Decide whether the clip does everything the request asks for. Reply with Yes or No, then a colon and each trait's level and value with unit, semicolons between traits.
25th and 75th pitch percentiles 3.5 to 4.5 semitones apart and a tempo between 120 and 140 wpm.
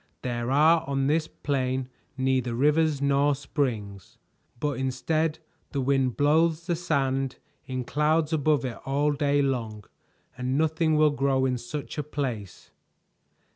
No: average, 2.8 semitones; slow, 135 wpm